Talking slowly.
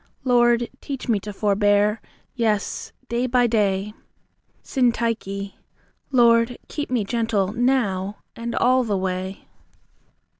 Yes: slow, 110 wpm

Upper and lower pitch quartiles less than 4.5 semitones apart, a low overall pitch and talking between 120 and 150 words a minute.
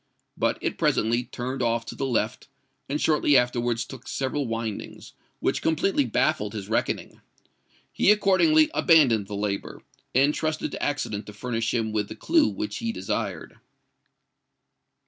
No: wide, 5.5 semitones; low, 125 Hz; average, 145 wpm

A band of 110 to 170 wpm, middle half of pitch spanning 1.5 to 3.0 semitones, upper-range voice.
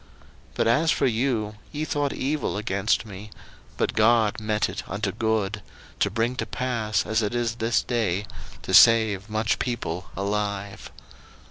No: average, 155 wpm; narrow, 2.4 semitones; low, 110 Hz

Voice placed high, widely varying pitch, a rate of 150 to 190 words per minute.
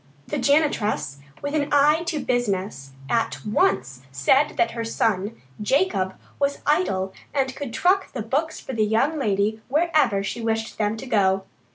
Yes: high, 230 Hz; wide, 6.2 semitones; average, 160 wpm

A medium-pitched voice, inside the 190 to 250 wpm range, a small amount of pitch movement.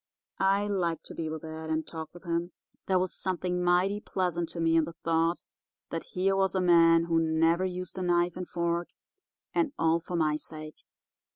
Yes: medium, 170 Hz; average, 195 wpm; narrow, 1.8 semitones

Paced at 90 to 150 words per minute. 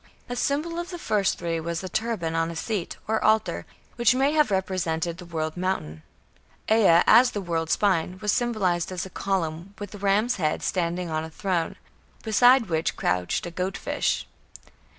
No: average, 175 wpm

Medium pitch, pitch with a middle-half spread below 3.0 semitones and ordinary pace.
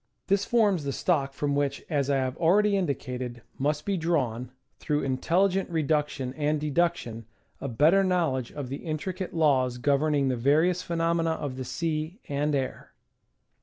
No: medium, 150 Hz; average, 4.0 semitones; average, 155 wpm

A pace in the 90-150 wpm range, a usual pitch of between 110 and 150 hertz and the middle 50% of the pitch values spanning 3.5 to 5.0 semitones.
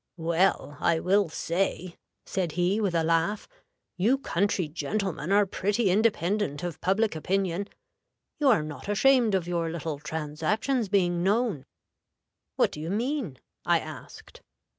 No: average, 140 wpm; medium, 185 Hz; average, 3.9 semitones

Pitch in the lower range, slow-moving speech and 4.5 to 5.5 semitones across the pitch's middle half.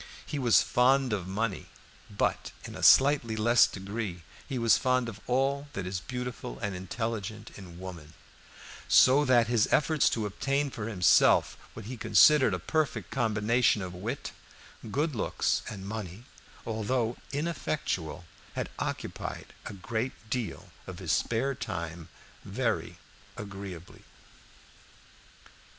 Yes: low, 110 Hz; slow, 130 wpm; average, 4.9 semitones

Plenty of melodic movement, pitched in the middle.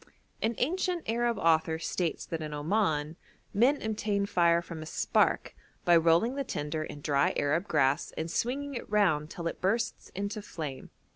Yes: wide, 5.9 semitones; medium, 170 Hz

